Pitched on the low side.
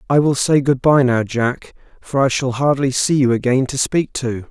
Yes: low, 130 Hz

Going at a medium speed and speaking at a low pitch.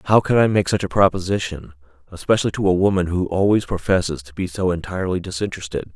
Yes: average, 190 wpm; very low, 90 Hz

